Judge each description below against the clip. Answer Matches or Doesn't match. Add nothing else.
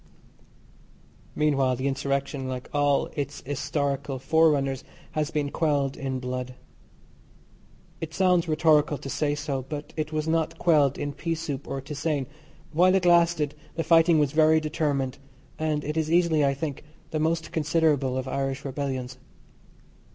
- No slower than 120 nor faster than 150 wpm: Matches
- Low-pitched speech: Doesn't match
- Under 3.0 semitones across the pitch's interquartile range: Matches